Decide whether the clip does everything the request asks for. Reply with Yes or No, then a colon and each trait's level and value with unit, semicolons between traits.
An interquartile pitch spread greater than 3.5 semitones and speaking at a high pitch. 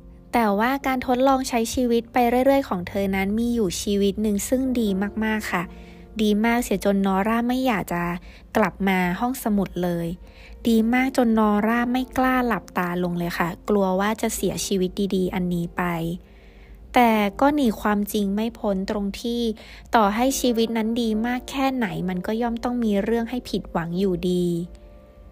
Yes: average, 4.2 semitones; high, 215 Hz